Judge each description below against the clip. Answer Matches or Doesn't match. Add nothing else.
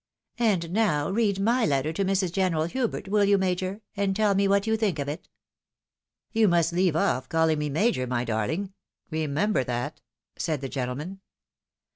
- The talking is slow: Doesn't match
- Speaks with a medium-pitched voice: Matches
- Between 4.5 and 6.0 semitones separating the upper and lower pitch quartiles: Matches